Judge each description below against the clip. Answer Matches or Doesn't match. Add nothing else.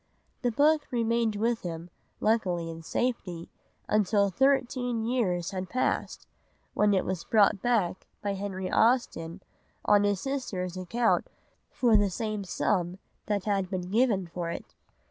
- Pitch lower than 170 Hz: Doesn't match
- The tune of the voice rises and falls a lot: Doesn't match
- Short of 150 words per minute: Matches